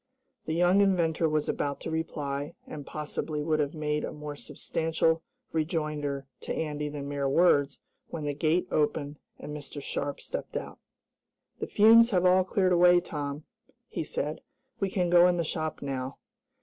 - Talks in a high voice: No, medium, 155 Hz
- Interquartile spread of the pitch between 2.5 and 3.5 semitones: Yes, average, 3.0 semitones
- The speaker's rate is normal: Yes, average, 165 wpm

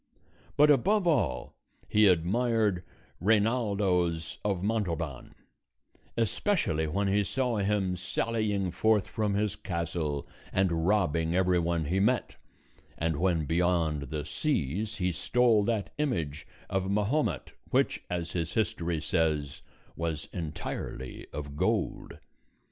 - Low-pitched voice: Yes, very low, 95 Hz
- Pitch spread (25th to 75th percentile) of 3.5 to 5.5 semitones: Yes, average, 4.7 semitones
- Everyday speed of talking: No, slow, 115 wpm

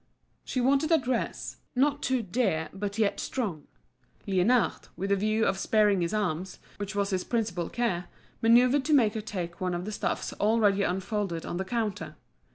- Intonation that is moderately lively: Yes, average, 4.0 semitones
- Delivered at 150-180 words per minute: Yes, average, 175 wpm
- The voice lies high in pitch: Yes, high, 210 Hz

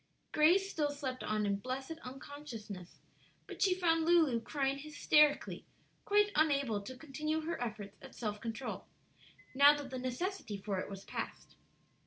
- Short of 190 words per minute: Yes, average, 150 wpm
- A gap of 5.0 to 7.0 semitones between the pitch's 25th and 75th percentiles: Yes, average, 5.3 semitones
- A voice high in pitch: Yes, very high, 275 Hz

